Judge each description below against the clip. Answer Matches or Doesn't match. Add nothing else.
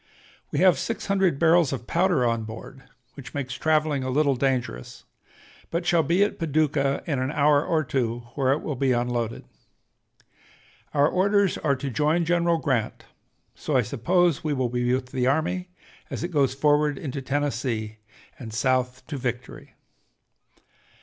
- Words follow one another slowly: Doesn't match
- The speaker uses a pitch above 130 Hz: Matches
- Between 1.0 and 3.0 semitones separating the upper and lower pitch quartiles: Doesn't match